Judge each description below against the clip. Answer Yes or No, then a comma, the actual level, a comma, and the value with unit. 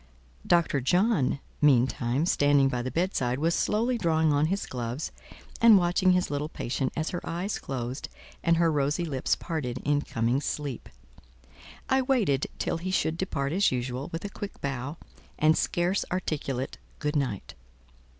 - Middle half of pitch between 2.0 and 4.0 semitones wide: No, average, 4.8 semitones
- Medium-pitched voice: Yes, medium, 150 Hz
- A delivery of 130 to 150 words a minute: No, average, 160 wpm